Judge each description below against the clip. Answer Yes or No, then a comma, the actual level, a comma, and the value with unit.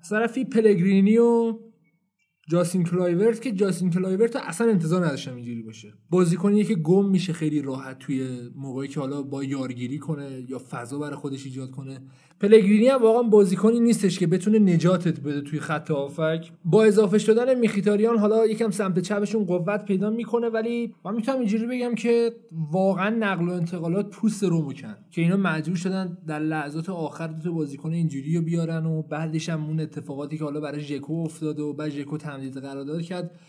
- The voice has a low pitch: No, medium, 175 Hz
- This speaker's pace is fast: Yes, fast, 175 wpm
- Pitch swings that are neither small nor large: No, wide, 5.9 semitones